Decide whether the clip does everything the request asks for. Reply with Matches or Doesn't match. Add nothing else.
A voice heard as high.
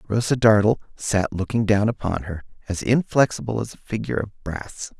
Doesn't match